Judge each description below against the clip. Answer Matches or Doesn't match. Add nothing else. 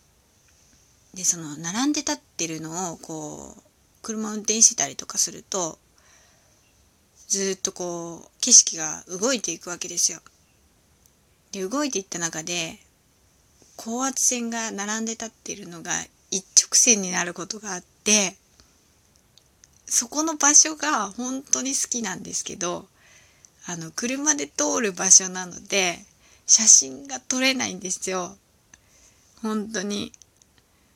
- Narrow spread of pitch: Doesn't match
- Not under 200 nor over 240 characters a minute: Matches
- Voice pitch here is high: Matches